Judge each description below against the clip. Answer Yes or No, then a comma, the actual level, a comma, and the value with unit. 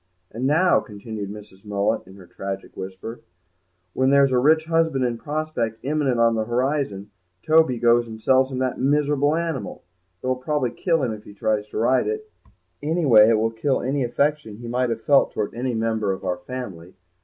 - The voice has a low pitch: Yes, low, 125 Hz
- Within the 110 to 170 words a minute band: No, average, 190 wpm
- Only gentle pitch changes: No, average, 4.7 semitones